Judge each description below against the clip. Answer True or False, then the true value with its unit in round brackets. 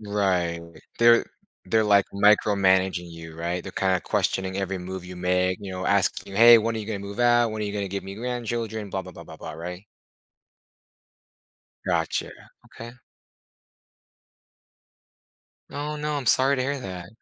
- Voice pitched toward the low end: True (100 Hz)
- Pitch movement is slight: False (3.8 semitones)